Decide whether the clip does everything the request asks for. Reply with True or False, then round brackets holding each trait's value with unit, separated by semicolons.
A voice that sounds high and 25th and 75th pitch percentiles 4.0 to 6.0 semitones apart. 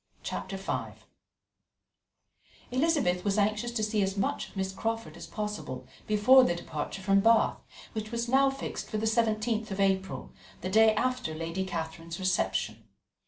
False (210 Hz; 3.2 semitones)